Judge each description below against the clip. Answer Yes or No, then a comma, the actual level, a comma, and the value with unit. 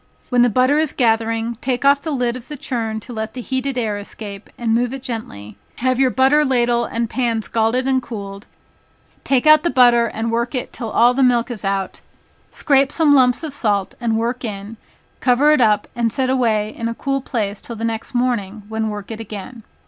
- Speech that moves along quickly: Yes, fast, 210 wpm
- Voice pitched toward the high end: Yes, high, 235 Hz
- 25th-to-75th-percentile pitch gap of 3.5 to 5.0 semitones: No, average, 2.7 semitones